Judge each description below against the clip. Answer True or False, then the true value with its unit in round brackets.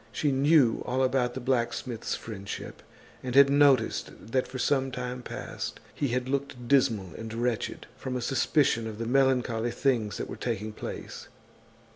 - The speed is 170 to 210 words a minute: False (160 wpm)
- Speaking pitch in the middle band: False (125 Hz)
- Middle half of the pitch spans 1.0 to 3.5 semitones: True (2.5 semitones)